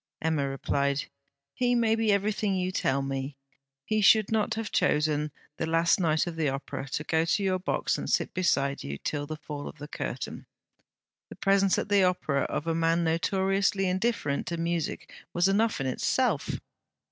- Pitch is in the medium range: Yes, medium, 165 Hz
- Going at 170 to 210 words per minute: Yes, average, 180 wpm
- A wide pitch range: No, average, 4.9 semitones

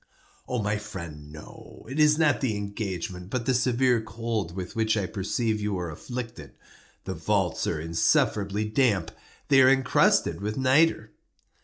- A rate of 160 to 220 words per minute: No, average, 150 wpm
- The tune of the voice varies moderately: Yes, average, 4.9 semitones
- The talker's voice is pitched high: No, low, 110 Hz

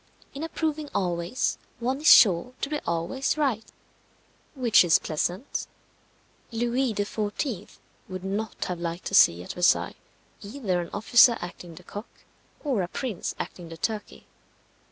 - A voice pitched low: No, high, 205 Hz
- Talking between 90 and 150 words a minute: Yes, average, 140 wpm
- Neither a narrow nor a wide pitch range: No, wide, 6.4 semitones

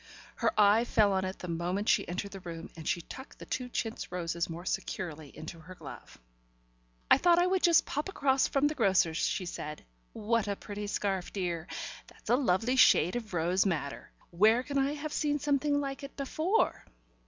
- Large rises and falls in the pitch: Yes, wide, 7.6 semitones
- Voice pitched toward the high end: Yes, high, 205 Hz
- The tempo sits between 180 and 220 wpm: Yes, average, 195 wpm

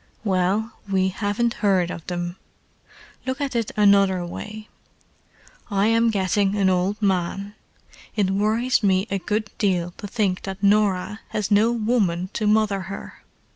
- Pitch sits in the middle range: No, high, 200 Hz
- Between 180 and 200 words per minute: No, average, 145 wpm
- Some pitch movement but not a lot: No, narrow, 2.3 semitones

